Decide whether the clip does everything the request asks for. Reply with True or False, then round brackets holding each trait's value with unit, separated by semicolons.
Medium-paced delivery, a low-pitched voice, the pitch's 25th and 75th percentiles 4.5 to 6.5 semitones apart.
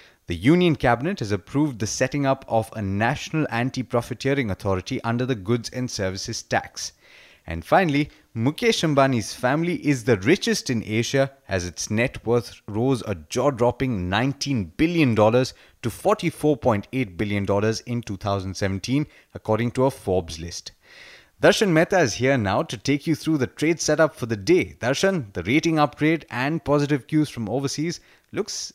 True (155 wpm; 125 Hz; 5.4 semitones)